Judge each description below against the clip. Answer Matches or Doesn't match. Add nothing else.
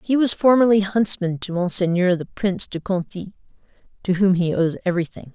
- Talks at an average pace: Matches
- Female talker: Matches